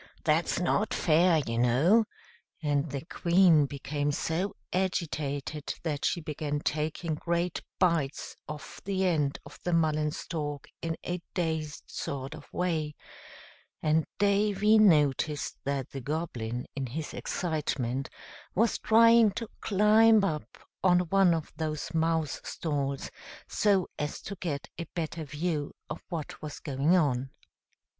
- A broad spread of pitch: No, average, 3.7 semitones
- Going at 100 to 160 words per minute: Yes, slow, 135 wpm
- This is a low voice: No, medium, 160 Hz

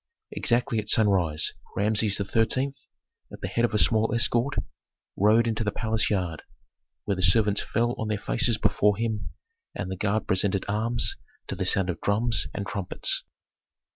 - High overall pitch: No, low, 105 Hz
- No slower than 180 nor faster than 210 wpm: No, average, 165 wpm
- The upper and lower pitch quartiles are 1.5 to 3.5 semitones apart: Yes, narrow, 2.5 semitones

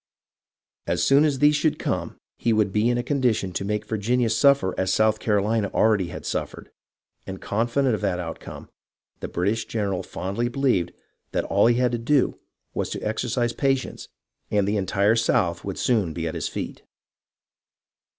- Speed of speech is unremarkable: Yes, average, 170 wpm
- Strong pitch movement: No, average, 3.7 semitones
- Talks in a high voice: No, low, 110 Hz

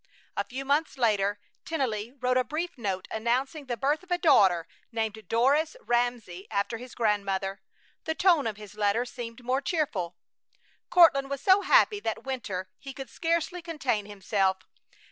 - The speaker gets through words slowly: No, average, 160 wpm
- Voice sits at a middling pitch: No, high, 245 Hz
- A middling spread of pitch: No, wide, 6.1 semitones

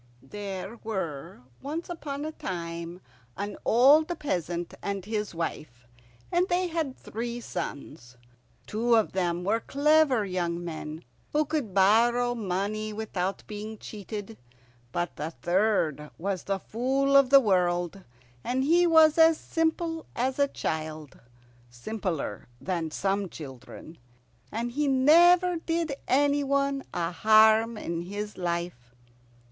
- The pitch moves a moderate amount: No, wide, 8.0 semitones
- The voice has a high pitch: Yes, high, 215 Hz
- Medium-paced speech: No, slow, 125 wpm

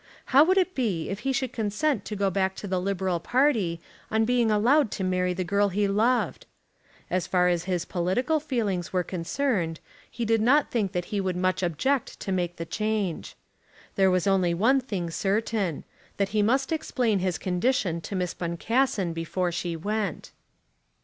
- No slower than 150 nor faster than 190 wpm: Yes, average, 180 wpm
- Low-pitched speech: No, high, 195 Hz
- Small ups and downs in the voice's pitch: No, average, 4.5 semitones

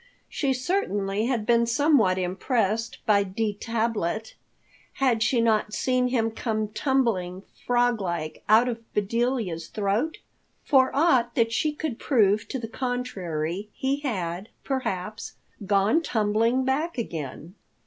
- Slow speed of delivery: Yes, slow, 130 wpm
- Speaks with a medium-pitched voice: No, high, 225 Hz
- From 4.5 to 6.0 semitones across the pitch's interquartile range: No, average, 4.1 semitones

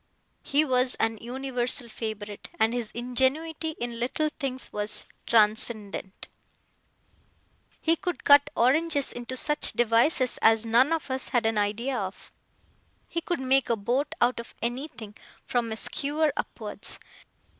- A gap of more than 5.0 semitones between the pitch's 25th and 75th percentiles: No, average, 3.8 semitones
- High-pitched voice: Yes, high, 245 Hz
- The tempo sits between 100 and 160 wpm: Yes, slow, 135 wpm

